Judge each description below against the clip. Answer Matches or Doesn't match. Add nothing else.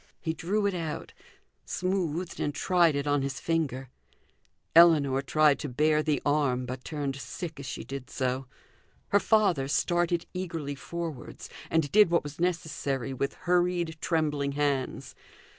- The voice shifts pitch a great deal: Doesn't match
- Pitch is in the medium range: Matches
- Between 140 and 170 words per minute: Matches